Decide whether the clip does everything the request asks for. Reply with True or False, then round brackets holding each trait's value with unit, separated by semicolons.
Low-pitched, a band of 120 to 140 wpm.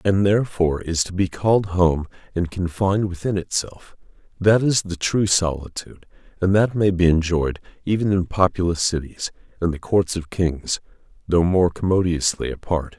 False (90 Hz; 155 wpm)